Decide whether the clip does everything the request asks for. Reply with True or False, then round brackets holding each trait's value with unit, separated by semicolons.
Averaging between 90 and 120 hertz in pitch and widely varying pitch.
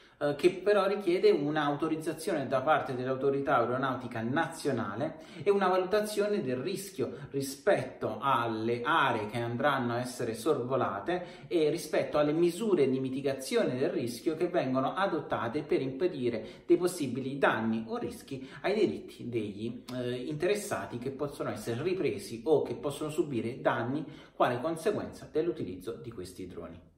False (140 Hz; 6.1 semitones)